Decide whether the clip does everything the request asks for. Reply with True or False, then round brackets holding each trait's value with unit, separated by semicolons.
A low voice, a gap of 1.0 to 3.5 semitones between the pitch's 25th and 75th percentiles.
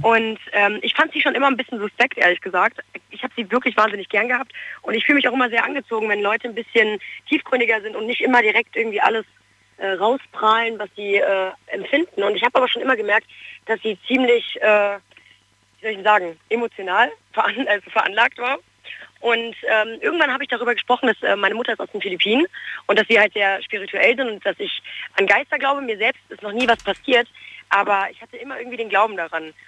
False (225 Hz; 3.1 semitones)